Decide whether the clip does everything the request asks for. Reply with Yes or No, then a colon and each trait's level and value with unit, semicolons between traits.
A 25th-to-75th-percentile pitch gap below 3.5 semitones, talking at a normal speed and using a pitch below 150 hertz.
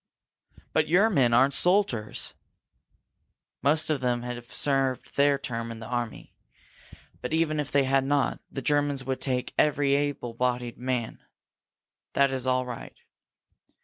Yes: average, 2.8 semitones; average, 145 wpm; low, 135 Hz